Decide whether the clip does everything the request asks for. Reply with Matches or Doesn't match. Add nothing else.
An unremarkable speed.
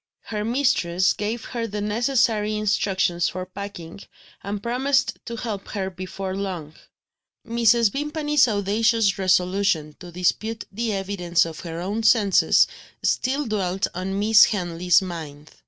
Doesn't match